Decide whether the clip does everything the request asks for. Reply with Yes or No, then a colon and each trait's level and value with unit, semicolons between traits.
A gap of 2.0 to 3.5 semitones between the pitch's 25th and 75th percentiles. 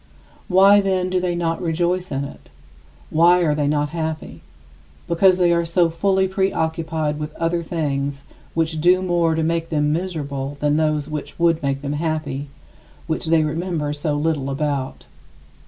Yes: average, 2.8 semitones